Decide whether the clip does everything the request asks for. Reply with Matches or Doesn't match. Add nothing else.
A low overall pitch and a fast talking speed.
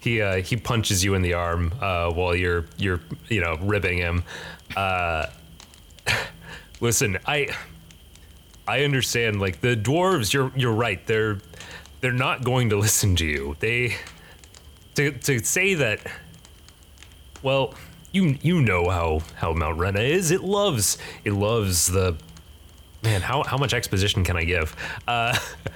Doesn't match